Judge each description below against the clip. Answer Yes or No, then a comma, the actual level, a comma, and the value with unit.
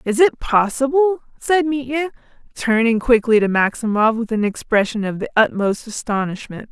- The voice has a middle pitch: No, high, 240 Hz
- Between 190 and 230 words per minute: No, average, 145 wpm